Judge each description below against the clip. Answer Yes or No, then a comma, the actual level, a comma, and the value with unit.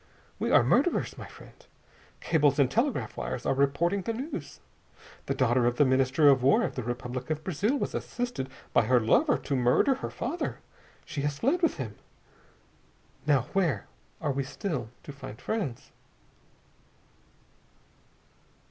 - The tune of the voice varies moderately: No, wide, 7.7 semitones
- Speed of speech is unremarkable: Yes, average, 150 wpm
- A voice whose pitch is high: No, medium, 140 Hz